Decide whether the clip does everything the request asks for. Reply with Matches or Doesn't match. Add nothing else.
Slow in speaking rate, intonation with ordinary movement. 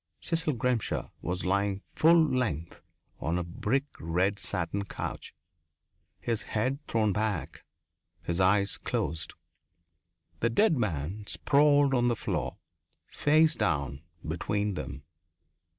Doesn't match